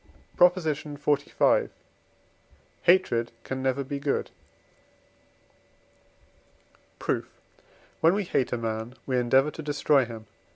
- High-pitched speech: No, medium, 140 Hz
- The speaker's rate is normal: No, slow, 110 wpm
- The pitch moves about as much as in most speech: Yes, average, 3.7 semitones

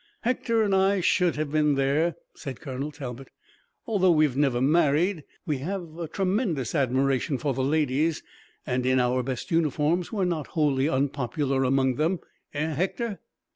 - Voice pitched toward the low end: No, medium, 150 Hz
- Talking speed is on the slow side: No, average, 155 wpm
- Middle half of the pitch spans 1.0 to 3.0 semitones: No, average, 4.3 semitones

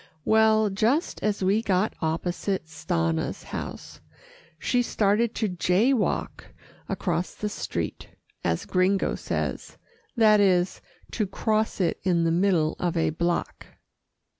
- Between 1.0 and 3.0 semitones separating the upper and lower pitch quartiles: No, average, 3.8 semitones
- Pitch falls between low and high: No, high, 195 Hz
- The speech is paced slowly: Yes, slow, 125 wpm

